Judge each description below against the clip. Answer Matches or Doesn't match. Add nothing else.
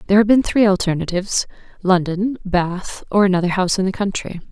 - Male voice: Doesn't match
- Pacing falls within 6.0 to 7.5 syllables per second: Matches